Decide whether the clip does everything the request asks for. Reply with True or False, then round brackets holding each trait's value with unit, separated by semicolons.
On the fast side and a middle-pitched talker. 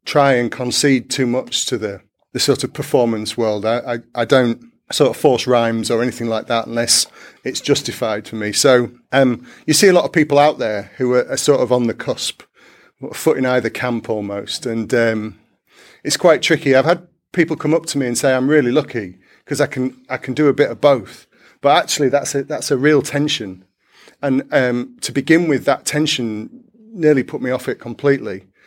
False (210 wpm; 130 Hz)